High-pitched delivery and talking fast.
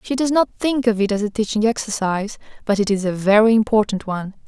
Yes: high, 215 Hz; fast, 230 wpm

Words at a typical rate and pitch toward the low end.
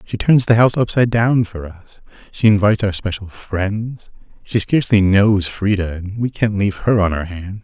Yes: average, 190 wpm; low, 105 Hz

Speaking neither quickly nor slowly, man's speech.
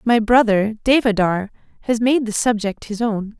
No: average, 160 wpm; female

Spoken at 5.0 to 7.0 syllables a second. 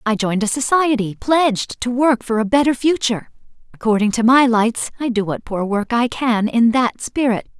Yes: 5.1 syllables/s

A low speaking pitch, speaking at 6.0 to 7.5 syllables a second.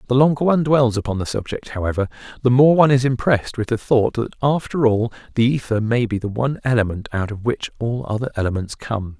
Yes: low, 120 Hz; 6.2 syllables/s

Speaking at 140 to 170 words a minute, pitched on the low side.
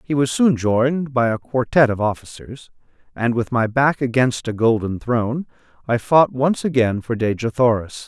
No: average, 180 wpm; low, 125 Hz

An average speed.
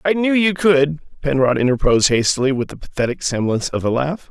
Yes: average, 195 wpm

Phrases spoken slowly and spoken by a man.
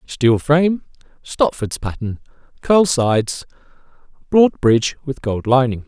Yes: slow, 110 wpm; male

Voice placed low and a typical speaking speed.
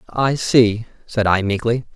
Yes: low, 115 Hz; average, 155 wpm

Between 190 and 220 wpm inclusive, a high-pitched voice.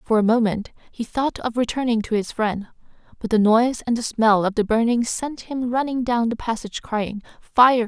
Yes: fast, 205 wpm; high, 230 Hz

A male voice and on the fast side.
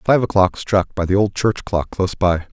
Yes: male; fast, 230 wpm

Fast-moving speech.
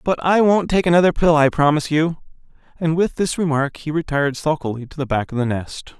Yes: fast, 220 wpm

